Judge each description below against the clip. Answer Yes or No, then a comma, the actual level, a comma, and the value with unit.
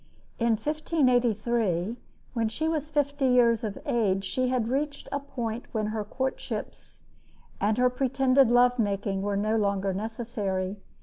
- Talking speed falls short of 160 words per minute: Yes, average, 140 wpm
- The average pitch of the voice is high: Yes, high, 235 Hz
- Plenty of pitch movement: No, average, 3.8 semitones